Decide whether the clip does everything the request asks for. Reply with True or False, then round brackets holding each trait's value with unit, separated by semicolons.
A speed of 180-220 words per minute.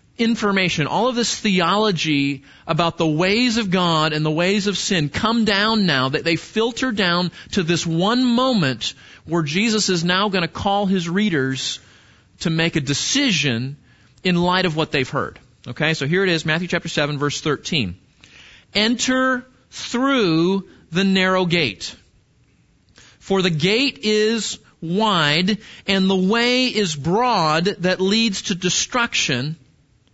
False (145 wpm)